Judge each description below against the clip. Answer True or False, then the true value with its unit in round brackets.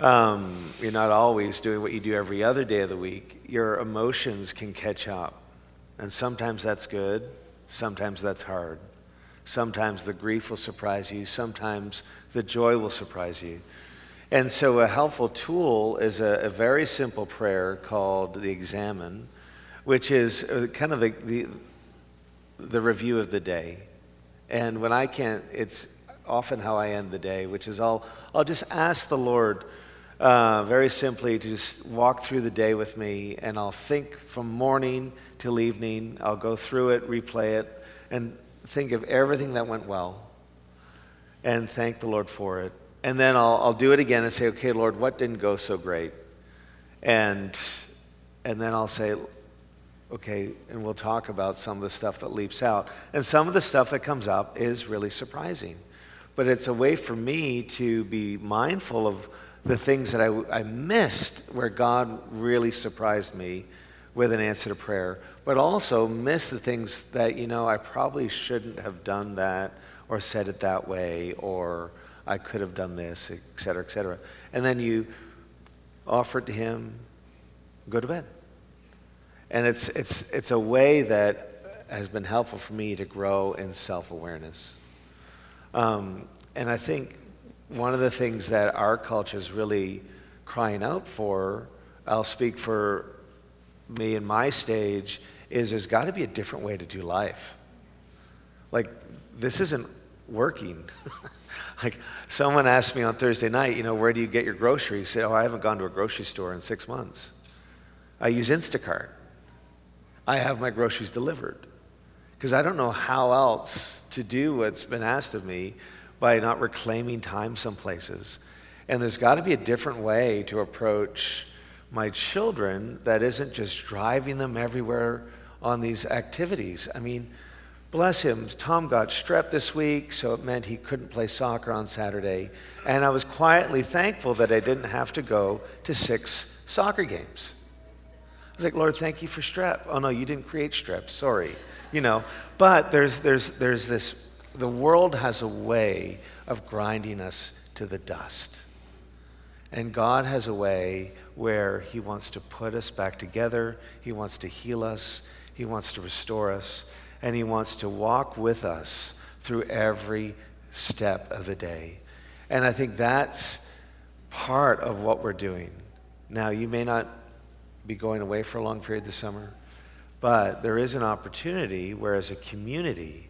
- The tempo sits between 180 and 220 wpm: False (170 wpm)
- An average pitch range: True (4.6 semitones)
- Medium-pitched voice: False (110 Hz)